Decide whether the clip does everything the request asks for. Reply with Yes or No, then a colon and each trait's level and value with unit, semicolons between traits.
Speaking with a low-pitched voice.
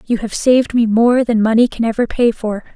No: high, 230 Hz